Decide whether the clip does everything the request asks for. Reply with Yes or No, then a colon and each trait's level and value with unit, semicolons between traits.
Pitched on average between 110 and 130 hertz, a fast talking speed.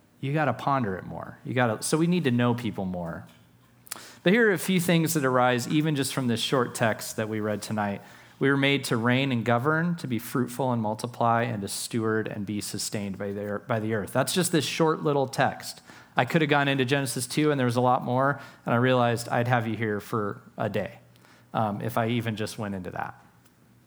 Yes: low, 120 Hz; fast, 230 wpm